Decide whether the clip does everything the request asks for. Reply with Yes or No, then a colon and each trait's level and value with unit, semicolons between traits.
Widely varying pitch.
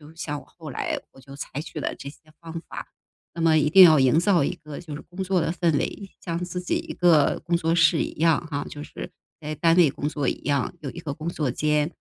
No: average, 2.7 semitones